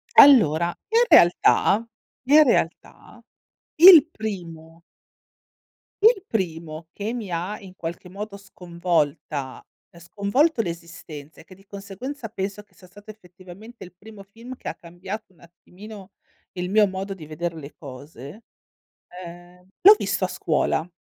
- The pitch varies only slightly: No, average, 4.2 semitones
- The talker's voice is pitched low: No, medium, 185 Hz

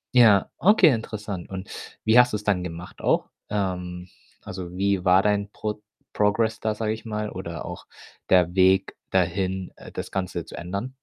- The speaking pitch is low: Yes, low, 100 Hz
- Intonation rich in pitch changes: No, average, 2.7 semitones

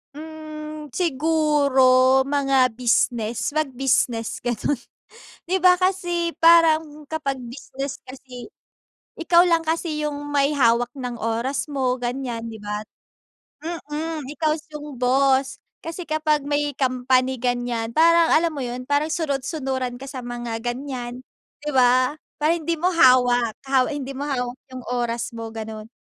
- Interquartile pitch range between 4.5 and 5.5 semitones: No, average, 3.8 semitones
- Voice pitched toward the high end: Yes, very high, 270 Hz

